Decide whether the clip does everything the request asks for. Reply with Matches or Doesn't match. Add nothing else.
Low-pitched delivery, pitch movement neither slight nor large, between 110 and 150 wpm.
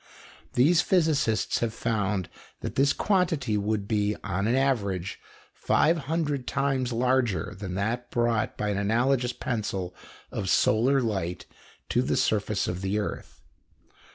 Matches